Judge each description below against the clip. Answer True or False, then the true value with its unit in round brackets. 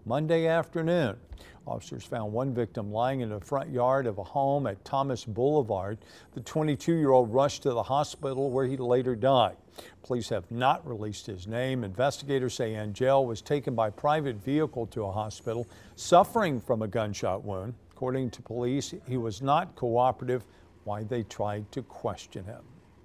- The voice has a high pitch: False (125 Hz)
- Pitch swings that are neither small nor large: True (3.9 semitones)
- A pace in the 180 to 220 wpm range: False (165 wpm)